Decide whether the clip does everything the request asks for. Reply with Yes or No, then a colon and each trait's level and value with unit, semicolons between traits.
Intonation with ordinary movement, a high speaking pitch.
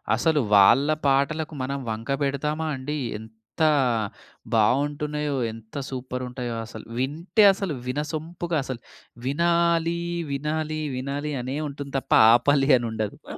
No: average, 3.4 semitones; medium, 145 Hz